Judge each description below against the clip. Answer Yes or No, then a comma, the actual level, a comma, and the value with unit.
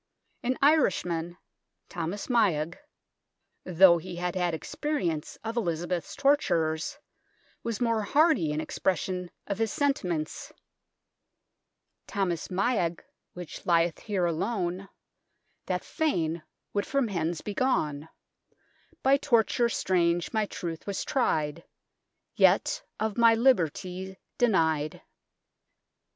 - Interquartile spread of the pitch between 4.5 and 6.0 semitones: Yes, wide, 5.4 semitones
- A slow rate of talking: Yes, slow, 110 wpm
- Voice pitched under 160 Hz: No, medium, 185 Hz